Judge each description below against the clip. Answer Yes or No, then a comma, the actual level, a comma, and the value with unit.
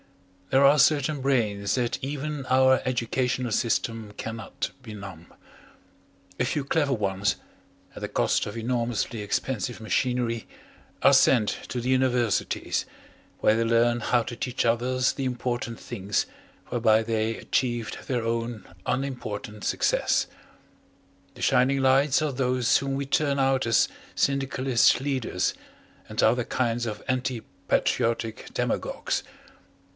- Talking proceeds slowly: Yes, slow, 125 wpm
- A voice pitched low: Yes, low, 120 Hz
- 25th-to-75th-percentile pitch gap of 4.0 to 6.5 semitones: No, average, 2.7 semitones